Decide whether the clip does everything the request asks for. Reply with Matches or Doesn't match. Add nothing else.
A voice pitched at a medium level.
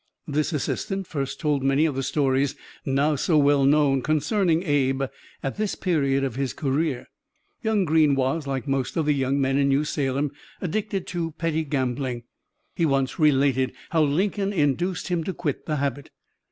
Matches